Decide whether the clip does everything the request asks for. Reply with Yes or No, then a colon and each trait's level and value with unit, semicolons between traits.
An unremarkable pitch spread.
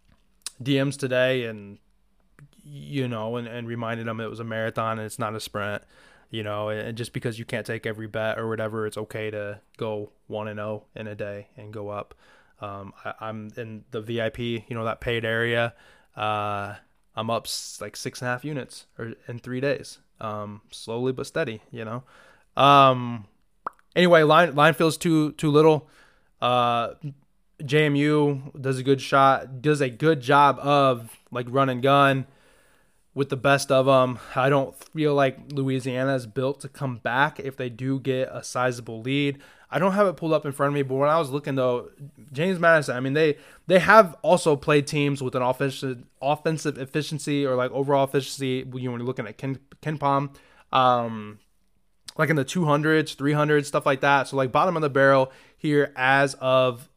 Yes: average, 3.6 semitones